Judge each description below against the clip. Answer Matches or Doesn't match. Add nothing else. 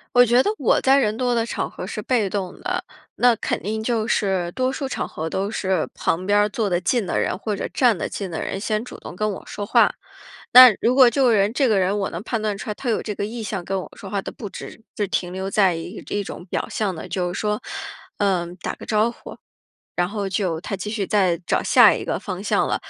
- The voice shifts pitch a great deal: Doesn't match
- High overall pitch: Matches